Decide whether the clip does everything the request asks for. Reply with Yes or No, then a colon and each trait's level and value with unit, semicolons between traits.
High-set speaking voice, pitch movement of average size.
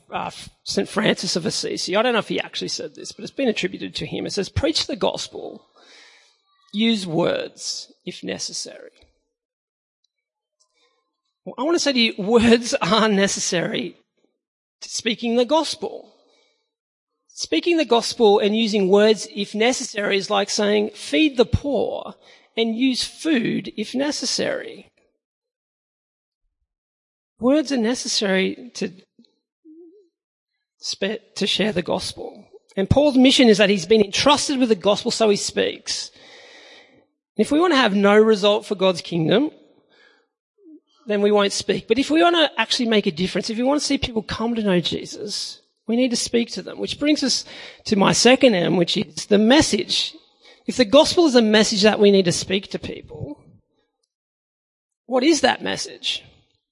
No: high, 235 Hz; wide, 7.0 semitones